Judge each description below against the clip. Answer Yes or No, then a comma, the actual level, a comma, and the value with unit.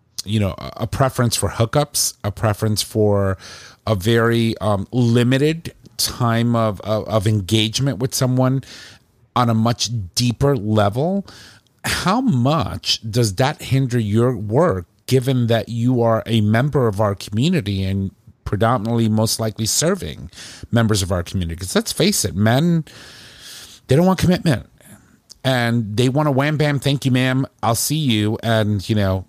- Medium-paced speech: Yes, average, 150 wpm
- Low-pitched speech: Yes, low, 115 Hz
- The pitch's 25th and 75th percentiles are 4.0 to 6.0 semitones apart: No, average, 3.3 semitones